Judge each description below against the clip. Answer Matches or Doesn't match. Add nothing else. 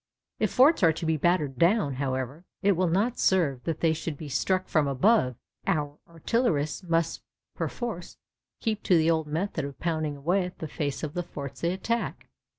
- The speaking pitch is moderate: Matches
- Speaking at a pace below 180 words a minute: Doesn't match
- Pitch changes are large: Doesn't match